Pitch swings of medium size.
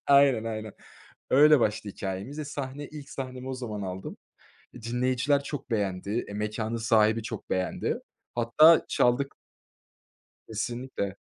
Yes: average, 4.3 semitones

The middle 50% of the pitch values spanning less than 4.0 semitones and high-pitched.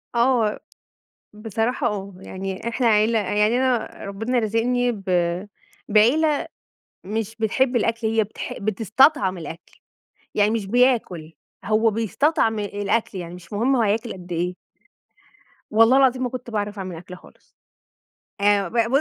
Yes: average, 3.2 semitones; high, 220 Hz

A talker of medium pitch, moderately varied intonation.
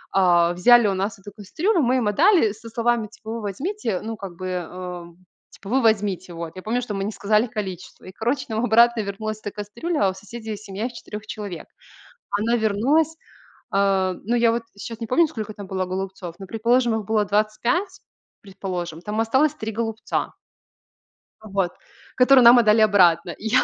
No: high, 215 Hz; average, 3.4 semitones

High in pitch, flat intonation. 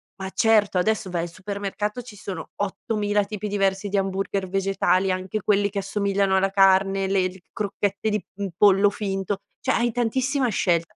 Yes: high, 195 Hz; narrow, 1.4 semitones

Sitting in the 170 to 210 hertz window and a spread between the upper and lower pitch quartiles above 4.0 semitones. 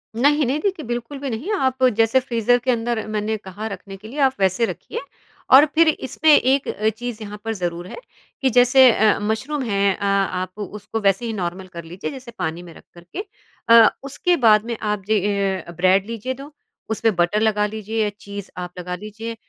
No: high, 220 Hz; average, 4.4 semitones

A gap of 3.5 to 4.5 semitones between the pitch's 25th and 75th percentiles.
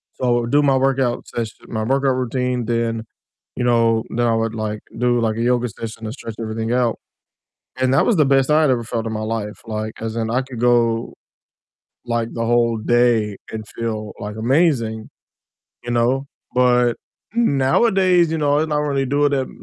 No: average, 2.7 semitones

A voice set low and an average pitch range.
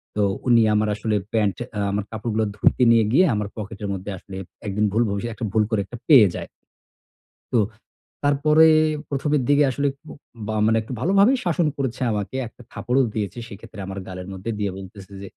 Yes: low, 110 Hz; average, 4.7 semitones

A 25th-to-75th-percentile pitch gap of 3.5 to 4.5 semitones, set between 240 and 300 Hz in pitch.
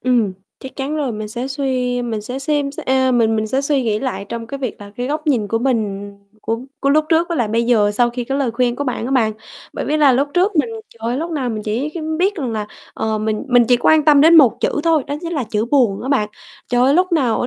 Yes: average, 4.2 semitones; very high, 255 Hz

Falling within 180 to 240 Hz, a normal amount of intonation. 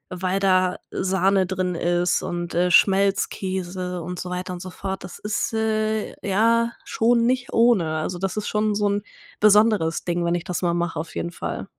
Yes: medium, 185 Hz; average, 3.0 semitones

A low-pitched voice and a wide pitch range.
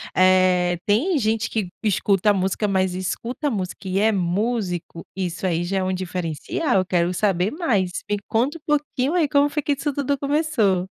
No: high, 195 Hz; wide, 6.0 semitones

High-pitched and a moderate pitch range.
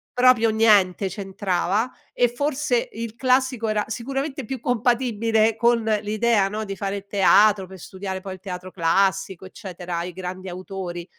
Yes: high, 205 Hz; average, 3.8 semitones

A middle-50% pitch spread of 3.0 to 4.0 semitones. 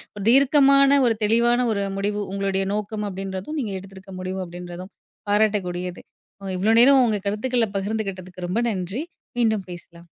Yes: average, 3.6 semitones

